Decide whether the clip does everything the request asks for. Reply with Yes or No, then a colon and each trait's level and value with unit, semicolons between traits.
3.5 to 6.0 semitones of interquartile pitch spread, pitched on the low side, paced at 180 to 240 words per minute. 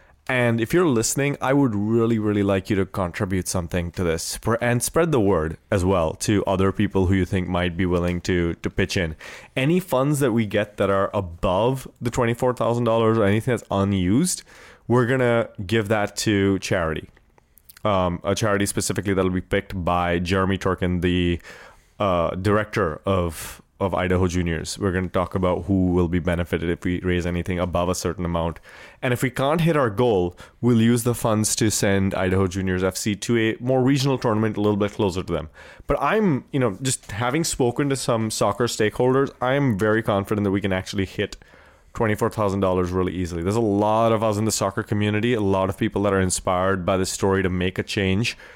Yes: average, 3.8 semitones; low, 100 Hz; fast, 205 wpm